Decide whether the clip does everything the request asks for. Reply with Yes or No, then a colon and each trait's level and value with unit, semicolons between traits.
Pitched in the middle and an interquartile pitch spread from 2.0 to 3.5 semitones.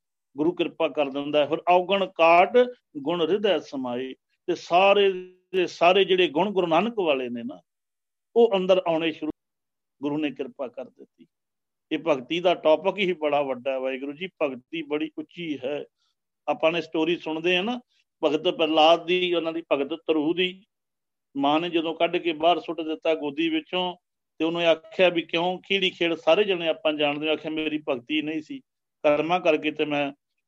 Yes: medium, 165 Hz; average, 2.9 semitones